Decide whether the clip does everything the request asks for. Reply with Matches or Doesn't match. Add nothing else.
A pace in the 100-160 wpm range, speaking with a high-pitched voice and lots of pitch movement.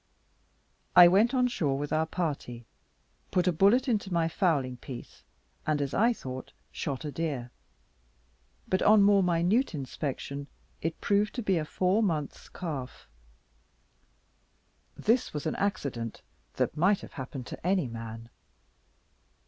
Doesn't match